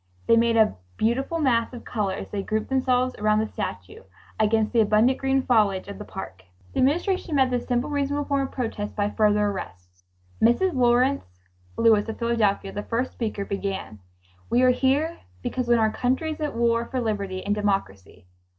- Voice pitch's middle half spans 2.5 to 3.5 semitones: No, average, 3.9 semitones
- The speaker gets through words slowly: No, average, 185 wpm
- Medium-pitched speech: No, high, 230 Hz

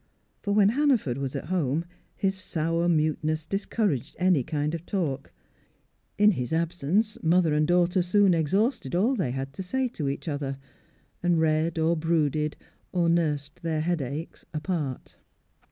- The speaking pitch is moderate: Yes, medium, 165 Hz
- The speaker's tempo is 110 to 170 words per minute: Yes, average, 150 wpm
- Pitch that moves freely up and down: No, average, 3.6 semitones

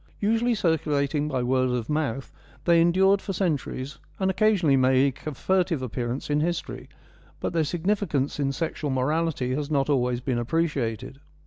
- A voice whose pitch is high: No, medium, 150 Hz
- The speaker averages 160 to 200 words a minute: No, average, 150 wpm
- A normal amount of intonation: Yes, average, 4.7 semitones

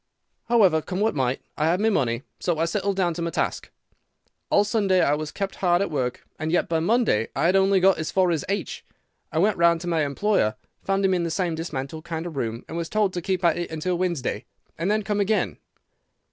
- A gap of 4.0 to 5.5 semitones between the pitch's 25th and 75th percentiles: No, average, 3.6 semitones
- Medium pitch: Yes, medium, 175 Hz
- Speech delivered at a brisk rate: Yes, fast, 230 wpm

